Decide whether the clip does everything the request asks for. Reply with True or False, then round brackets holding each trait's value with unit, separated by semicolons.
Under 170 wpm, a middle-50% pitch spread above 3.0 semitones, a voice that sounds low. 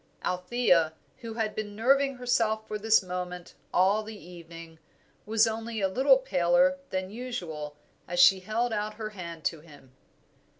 False (155 wpm; 4.3 semitones; 210 Hz)